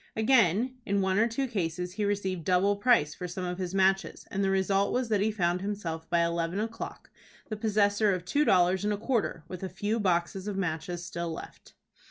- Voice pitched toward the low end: No, high, 195 Hz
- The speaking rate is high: Yes, fast, 210 wpm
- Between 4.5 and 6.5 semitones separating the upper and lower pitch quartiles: No, average, 2.9 semitones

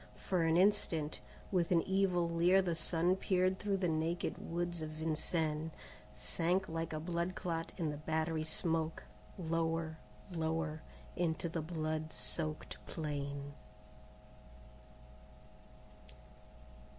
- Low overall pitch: No, medium, 165 Hz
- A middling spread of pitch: No, narrow, 1.8 semitones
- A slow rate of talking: Yes, slow, 115 wpm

